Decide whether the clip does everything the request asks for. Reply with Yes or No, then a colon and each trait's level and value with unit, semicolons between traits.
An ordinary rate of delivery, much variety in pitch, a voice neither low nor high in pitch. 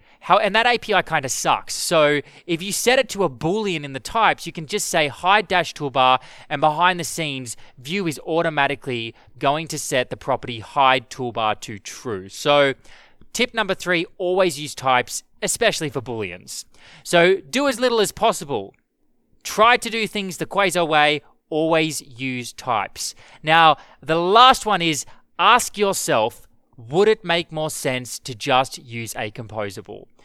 Yes: average, 165 wpm; wide, 6.3 semitones; medium, 155 Hz